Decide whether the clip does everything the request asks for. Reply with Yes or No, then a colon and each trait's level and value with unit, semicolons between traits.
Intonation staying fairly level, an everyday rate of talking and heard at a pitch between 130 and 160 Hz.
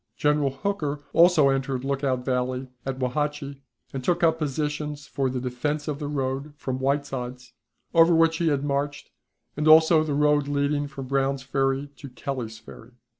Yes: narrow, 2.0 semitones; average, 165 wpm; medium, 140 Hz